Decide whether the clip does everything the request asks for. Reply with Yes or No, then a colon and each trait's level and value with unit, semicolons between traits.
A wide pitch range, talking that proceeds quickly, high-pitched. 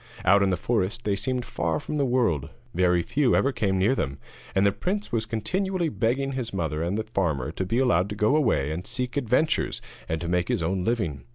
No: wide, 6.2 semitones; fast, 220 wpm; low, 105 Hz